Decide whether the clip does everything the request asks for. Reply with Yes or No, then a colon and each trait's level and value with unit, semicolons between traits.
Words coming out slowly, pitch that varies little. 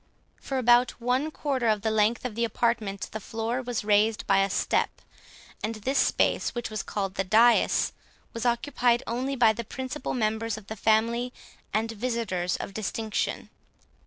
No: average, 165 wpm; narrow, 2.2 semitones